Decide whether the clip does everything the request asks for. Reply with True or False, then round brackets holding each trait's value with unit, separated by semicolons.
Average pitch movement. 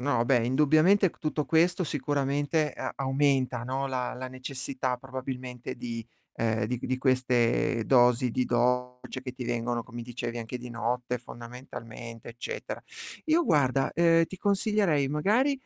True (3.1 semitones)